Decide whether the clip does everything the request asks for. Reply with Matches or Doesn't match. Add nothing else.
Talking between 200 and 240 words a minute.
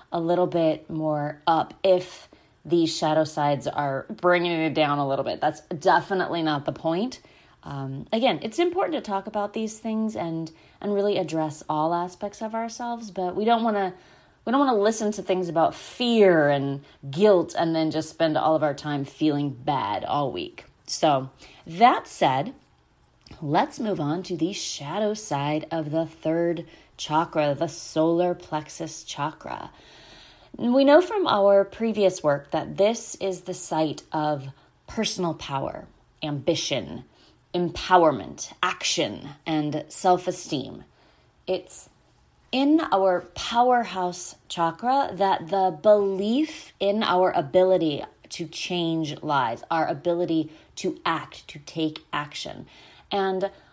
Doesn't match